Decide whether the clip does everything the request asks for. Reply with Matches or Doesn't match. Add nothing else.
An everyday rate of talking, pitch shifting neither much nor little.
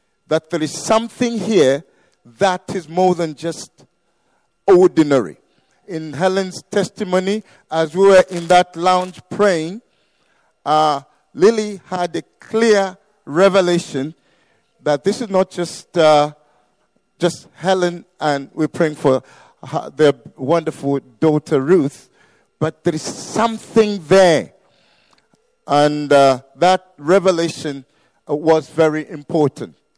Doesn't match